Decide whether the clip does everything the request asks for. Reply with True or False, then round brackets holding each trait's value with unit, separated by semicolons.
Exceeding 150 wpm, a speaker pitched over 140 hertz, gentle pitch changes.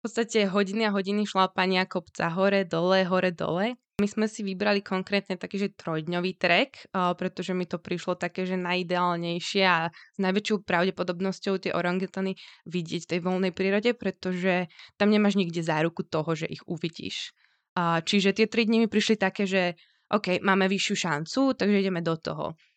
True (165 wpm; 190 Hz; 2.2 semitones)